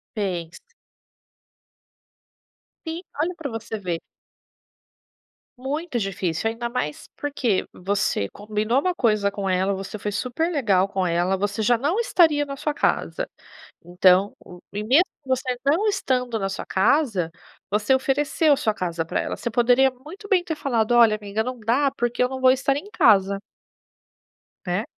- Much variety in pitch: Yes, wide, 5.8 semitones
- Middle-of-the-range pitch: No, high, 235 Hz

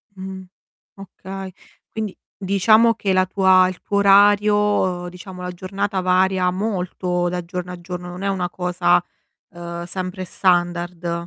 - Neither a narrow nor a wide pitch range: No, narrow, 1.6 semitones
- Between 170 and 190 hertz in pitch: Yes, medium, 185 Hz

